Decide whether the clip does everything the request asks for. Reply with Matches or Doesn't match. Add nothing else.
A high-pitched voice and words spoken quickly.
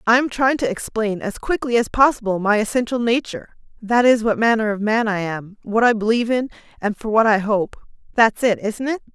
Matches